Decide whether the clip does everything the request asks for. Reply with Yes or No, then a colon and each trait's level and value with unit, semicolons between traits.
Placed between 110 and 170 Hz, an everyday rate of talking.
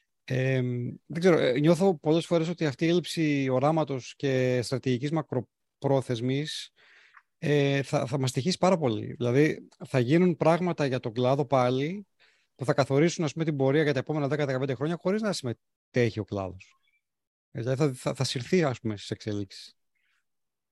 Yes: medium, 140 Hz; average, 160 wpm